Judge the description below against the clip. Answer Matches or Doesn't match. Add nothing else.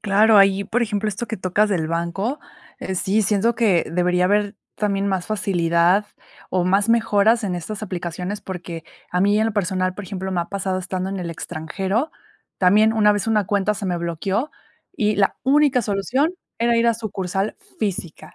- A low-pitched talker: Doesn't match